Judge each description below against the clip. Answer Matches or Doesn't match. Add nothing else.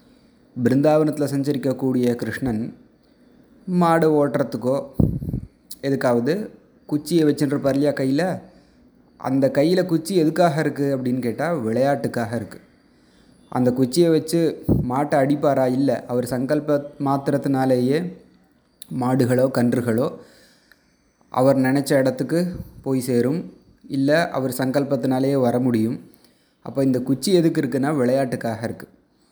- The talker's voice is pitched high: Doesn't match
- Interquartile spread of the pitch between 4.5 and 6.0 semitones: Doesn't match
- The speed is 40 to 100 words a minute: Matches